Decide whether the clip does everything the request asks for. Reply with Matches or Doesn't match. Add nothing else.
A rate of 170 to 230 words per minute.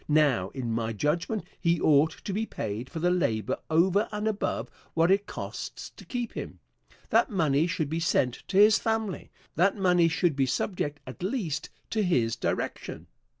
Matches